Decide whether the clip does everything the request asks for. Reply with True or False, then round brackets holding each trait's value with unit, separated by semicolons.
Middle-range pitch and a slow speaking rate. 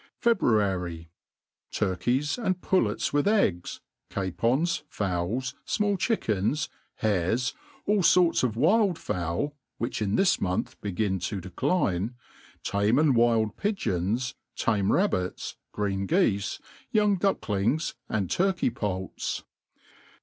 False (115 Hz; 105 wpm)